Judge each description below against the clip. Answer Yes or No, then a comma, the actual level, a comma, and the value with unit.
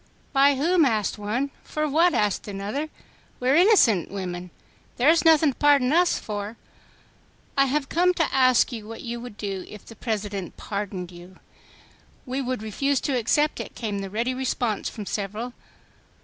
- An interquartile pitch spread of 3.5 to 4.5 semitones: No, wide, 5.5 semitones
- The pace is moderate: Yes, average, 170 wpm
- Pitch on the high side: Yes, high, 240 Hz